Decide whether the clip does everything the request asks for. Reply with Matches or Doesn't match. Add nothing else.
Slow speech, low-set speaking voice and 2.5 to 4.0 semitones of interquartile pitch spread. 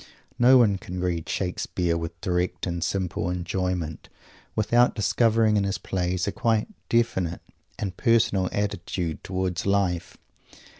Matches